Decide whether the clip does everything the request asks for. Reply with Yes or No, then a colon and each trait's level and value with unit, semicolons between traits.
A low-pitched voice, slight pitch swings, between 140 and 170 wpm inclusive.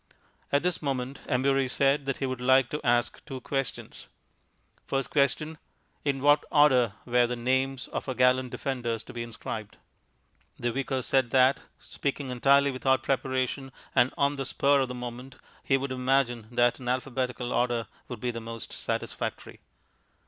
Yes: low, 130 Hz; narrow, 1.9 semitones; average, 165 wpm